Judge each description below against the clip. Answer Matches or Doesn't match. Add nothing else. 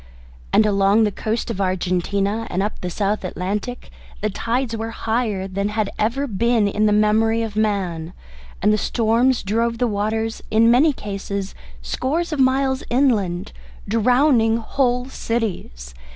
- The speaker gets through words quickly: Doesn't match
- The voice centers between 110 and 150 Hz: Doesn't match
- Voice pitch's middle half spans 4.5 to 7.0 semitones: Doesn't match